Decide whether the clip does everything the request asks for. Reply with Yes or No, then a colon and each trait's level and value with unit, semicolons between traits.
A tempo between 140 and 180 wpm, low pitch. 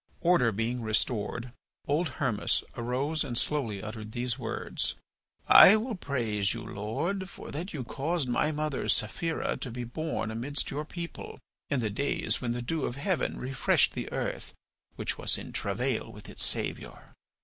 Yes: average, 160 wpm; low, 130 Hz